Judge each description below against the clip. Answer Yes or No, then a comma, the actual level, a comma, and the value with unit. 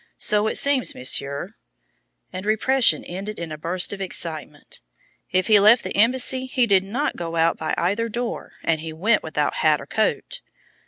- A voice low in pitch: No, high, 200 Hz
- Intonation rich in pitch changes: Yes, wide, 5.7 semitones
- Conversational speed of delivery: Yes, average, 175 wpm